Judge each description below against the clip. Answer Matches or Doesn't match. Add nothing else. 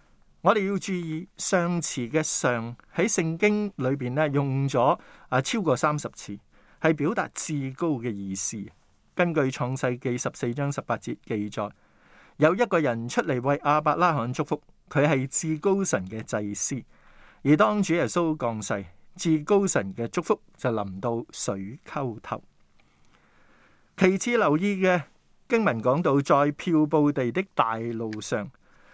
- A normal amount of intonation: Doesn't match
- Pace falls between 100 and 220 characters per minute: Matches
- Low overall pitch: Doesn't match